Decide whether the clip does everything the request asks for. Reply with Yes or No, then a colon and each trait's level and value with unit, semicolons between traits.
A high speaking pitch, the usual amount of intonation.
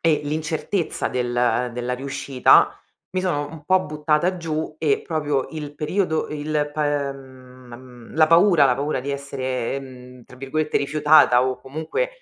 No: medium, 145 Hz; average, 3.2 semitones